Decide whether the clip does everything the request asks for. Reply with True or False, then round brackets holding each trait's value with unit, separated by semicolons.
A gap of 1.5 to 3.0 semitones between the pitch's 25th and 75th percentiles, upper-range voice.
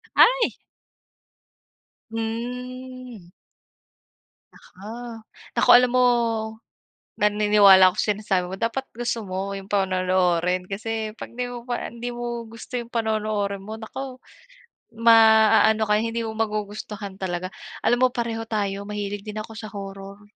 True (2.7 semitones; 215 Hz)